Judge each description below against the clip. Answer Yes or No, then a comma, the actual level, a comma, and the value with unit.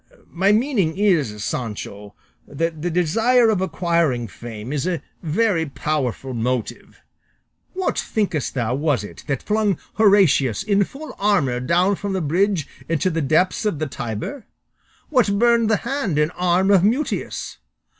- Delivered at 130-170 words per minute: Yes, average, 145 wpm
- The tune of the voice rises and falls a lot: Yes, wide, 6.8 semitones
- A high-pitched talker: No, medium, 175 Hz